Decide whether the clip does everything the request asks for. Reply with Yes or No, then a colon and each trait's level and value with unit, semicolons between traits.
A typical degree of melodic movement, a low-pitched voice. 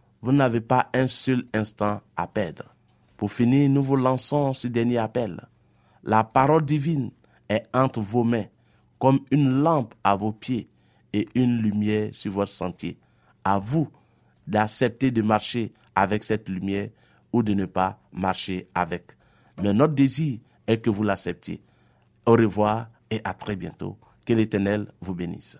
Yes: average, 3.8 semitones; low, 115 Hz